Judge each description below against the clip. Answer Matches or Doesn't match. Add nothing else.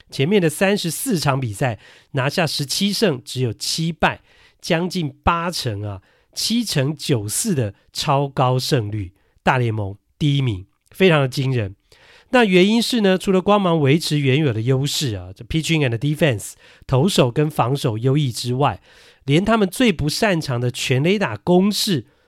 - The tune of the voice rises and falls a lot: Matches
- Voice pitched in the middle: Matches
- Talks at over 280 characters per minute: Doesn't match